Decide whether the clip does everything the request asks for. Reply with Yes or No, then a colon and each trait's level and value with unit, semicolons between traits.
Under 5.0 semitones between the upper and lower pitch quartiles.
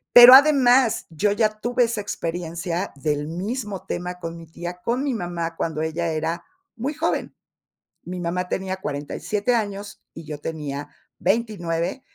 No: wide, 5.6 semitones